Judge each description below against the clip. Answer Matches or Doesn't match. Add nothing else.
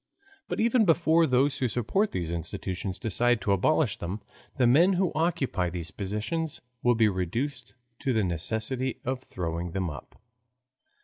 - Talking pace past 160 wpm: Doesn't match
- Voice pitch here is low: Matches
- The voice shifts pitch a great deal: Matches